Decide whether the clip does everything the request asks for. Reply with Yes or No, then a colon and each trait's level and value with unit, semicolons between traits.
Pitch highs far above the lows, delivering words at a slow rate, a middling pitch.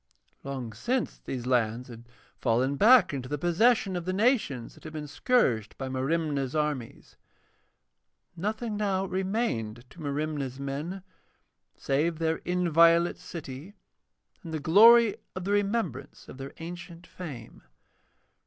Yes: wide, 6.0 semitones; slow, 130 wpm; medium, 160 Hz